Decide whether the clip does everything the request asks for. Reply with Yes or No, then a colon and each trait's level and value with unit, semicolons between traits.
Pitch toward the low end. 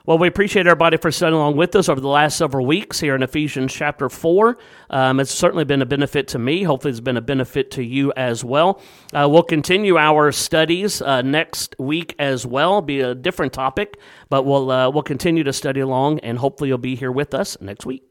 No: medium, 145 Hz